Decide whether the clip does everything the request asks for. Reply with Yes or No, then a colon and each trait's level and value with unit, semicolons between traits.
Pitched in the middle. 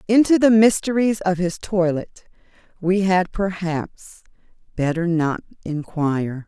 Yes: medium, 180 Hz